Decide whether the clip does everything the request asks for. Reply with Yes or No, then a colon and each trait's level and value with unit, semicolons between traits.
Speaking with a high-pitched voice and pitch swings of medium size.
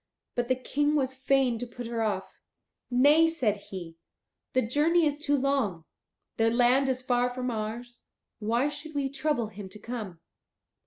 Yes: very high, 250 Hz; average, 3.8 semitones